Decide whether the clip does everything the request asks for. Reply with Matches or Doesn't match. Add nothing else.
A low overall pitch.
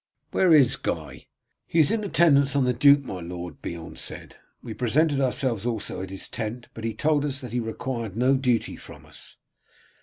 Matches